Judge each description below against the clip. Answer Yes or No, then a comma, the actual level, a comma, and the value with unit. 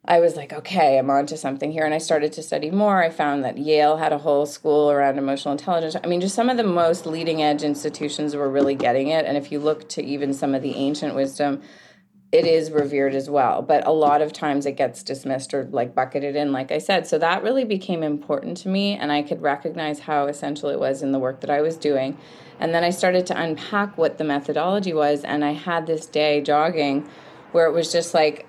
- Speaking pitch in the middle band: Yes, medium, 150 Hz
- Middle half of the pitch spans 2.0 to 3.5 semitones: Yes, narrow, 2.5 semitones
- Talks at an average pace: No, fast, 240 wpm